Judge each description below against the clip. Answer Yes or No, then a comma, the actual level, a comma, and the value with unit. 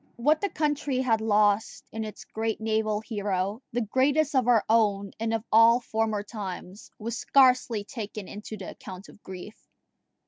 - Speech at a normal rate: Yes, average, 165 wpm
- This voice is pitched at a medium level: No, high, 220 Hz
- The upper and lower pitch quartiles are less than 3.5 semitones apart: Yes, average, 2.7 semitones